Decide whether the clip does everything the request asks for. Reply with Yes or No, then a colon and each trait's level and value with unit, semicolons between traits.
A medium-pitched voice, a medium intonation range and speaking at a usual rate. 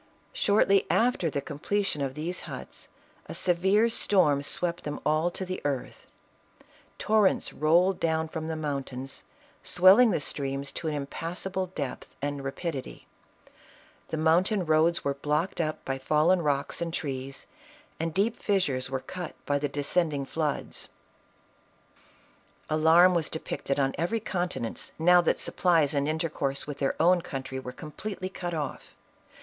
Yes: medium, 160 Hz; average, 4.1 semitones; average, 145 wpm